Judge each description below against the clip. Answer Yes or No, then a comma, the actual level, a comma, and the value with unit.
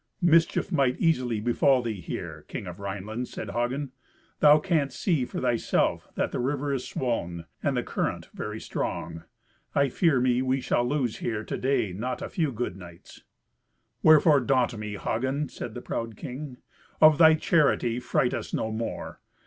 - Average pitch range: Yes, average, 4.1 semitones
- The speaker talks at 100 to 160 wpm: No, average, 170 wpm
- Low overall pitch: Yes, low, 125 Hz